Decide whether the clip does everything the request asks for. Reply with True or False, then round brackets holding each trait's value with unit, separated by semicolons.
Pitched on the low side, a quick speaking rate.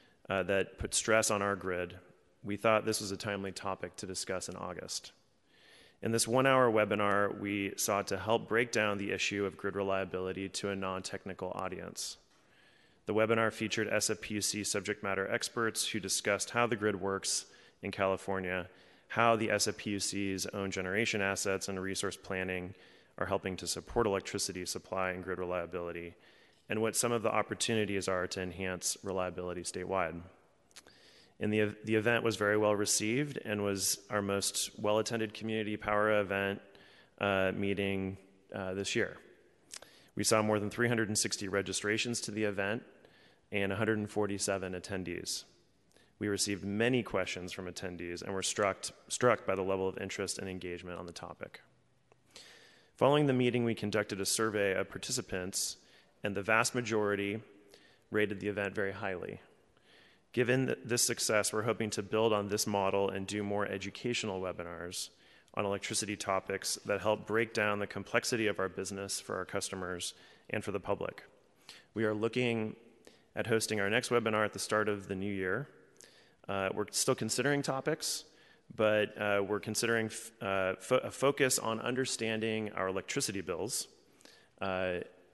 False (100 Hz; 155 wpm)